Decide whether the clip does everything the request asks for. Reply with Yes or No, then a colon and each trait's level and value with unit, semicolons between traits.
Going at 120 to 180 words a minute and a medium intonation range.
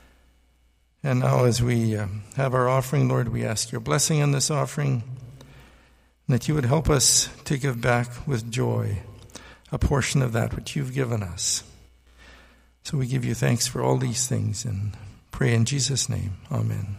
Yes: average, 175 wpm; average, 4.2 semitones